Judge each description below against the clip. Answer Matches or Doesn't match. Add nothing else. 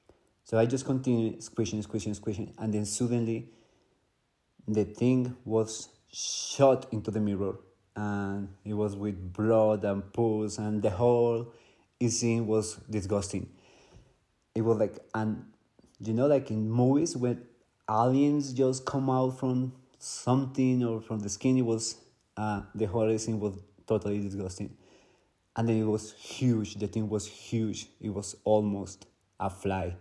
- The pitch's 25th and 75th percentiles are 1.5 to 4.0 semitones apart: Matches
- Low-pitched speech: Matches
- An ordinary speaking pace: Matches